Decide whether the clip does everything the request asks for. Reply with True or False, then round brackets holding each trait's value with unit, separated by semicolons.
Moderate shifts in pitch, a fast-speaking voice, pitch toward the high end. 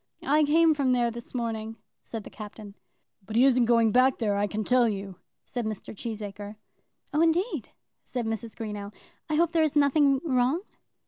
False (4.5 semitones; 180 wpm; 235 Hz)